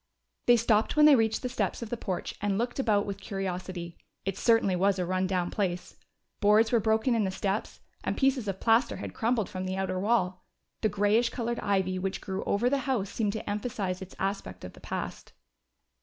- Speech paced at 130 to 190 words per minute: No, fast, 205 wpm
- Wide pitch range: No, average, 3.4 semitones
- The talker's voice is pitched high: Yes, high, 205 Hz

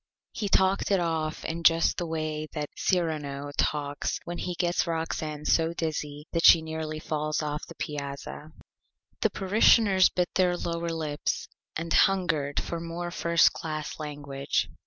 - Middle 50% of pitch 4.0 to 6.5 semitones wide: No, narrow, 2.4 semitones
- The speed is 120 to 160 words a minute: Yes, average, 150 wpm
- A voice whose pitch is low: No, medium, 160 Hz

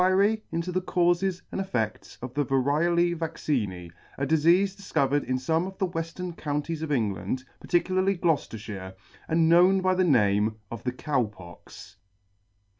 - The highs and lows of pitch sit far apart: Yes, wide, 6.0 semitones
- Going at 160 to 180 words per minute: No, average, 150 wpm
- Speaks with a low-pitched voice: No, medium, 160 Hz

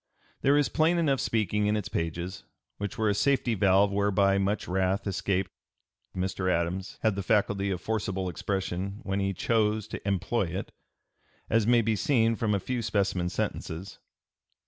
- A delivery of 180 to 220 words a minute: No, average, 165 wpm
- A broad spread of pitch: No, narrow, 2.6 semitones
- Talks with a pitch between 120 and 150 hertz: No, low, 100 Hz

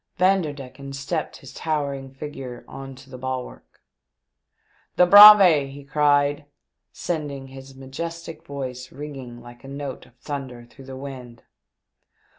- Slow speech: Yes, slow, 130 wpm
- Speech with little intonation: Yes, narrow, 2.2 semitones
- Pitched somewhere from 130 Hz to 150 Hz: Yes, low, 135 Hz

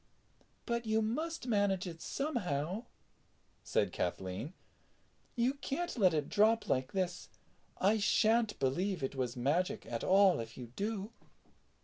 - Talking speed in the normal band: No, slow, 130 wpm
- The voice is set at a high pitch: Yes, high, 195 Hz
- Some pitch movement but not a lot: No, wide, 8.0 semitones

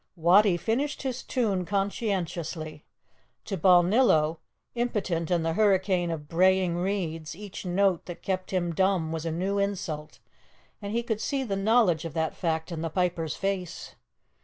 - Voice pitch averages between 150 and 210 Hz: Yes, medium, 185 Hz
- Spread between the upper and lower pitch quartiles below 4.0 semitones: Yes, average, 3.4 semitones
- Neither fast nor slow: Yes, average, 155 wpm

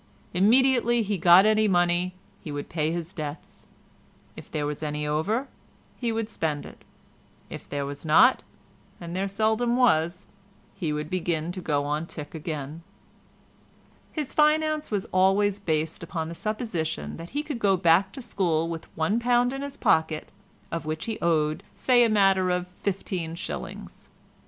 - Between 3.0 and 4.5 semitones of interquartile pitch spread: No, wide, 5.4 semitones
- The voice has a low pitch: No, medium, 180 Hz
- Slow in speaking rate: No, average, 150 wpm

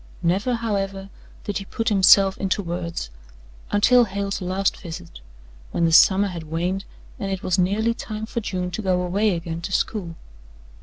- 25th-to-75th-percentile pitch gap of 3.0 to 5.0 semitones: No, narrow, 2.5 semitones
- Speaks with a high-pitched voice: Yes, high, 195 Hz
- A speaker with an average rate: Yes, average, 165 wpm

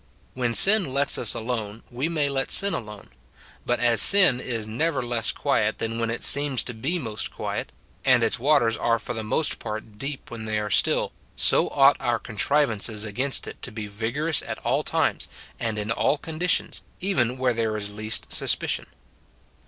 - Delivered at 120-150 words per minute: No, average, 185 wpm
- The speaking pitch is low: Yes, low, 120 Hz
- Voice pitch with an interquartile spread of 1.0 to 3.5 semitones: No, average, 4.1 semitones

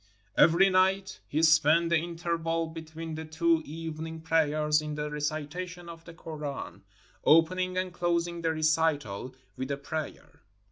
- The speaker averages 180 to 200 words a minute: No, average, 140 wpm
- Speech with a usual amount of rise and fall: No, narrow, 1.7 semitones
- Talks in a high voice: No, medium, 160 Hz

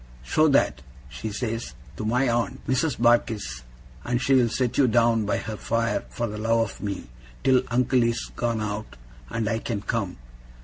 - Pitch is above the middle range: No, low, 115 Hz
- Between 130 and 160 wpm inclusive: No, average, 175 wpm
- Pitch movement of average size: No, narrow, 2.3 semitones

